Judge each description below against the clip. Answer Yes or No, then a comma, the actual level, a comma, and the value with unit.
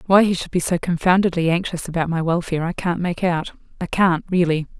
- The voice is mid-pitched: Yes, medium, 175 Hz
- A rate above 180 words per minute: Yes, average, 200 wpm